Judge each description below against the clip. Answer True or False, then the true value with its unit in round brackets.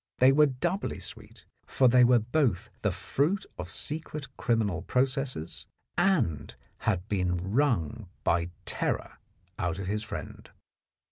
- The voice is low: True (115 Hz)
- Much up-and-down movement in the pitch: True (6.8 semitones)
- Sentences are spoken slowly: True (130 wpm)